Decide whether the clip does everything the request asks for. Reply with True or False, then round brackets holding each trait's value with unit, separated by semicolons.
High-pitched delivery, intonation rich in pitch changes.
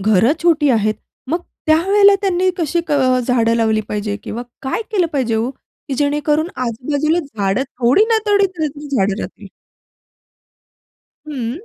True (280 Hz; 6.1 semitones)